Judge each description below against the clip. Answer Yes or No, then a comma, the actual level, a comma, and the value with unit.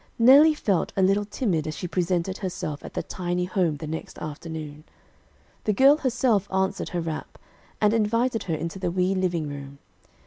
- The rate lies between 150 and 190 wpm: Yes, average, 175 wpm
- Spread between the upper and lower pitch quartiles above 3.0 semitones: Yes, average, 4.4 semitones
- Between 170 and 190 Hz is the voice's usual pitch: Yes, medium, 185 Hz